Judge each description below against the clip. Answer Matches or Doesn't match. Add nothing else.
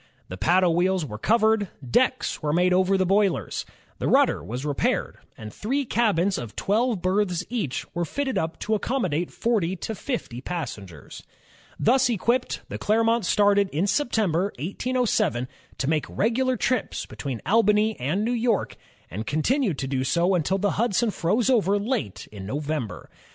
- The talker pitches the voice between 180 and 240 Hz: Matches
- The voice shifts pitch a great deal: Matches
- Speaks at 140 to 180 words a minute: Matches